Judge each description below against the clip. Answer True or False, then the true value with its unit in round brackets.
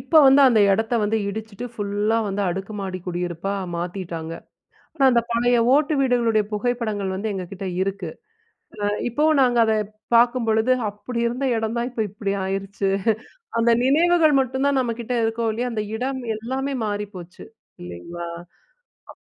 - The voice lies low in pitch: False (220 Hz)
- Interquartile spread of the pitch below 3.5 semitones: False (4.0 semitones)